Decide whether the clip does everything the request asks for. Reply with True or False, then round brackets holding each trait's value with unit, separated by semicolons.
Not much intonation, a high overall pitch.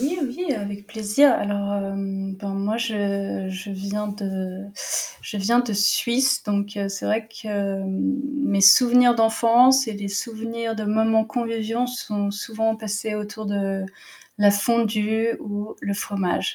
True (2.3 semitones; 210 Hz)